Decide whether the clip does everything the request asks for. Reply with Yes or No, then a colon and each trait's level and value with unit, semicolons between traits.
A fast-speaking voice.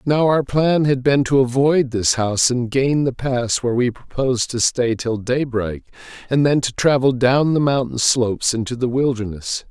No: average, 190 wpm